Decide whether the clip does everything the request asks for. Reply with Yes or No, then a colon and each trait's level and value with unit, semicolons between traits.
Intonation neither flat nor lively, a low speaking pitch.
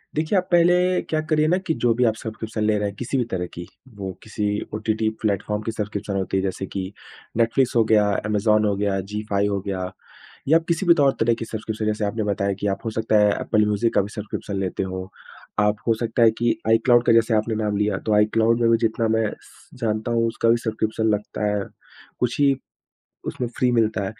No: narrow, 2.1 semitones; low, 110 Hz